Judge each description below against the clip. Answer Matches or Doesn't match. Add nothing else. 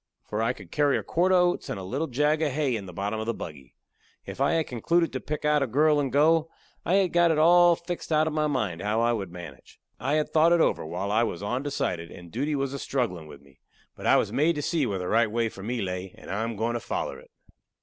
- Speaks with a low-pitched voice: Matches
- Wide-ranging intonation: Matches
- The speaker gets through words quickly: Matches